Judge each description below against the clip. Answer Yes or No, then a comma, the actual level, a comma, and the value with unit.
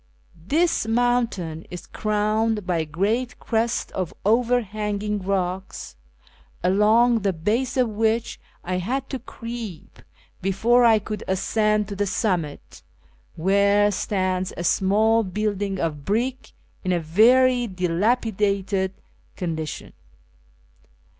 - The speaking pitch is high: Yes, high, 210 Hz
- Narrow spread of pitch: No, average, 3.5 semitones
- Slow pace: Yes, slow, 110 wpm